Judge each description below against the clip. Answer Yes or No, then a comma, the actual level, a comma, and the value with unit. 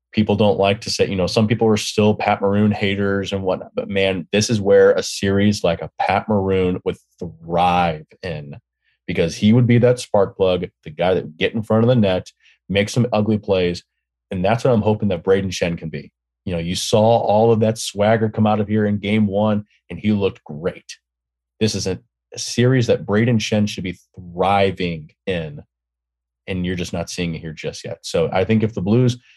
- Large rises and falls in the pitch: No, average, 3.3 semitones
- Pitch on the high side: No, low, 100 Hz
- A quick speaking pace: Yes, fast, 215 wpm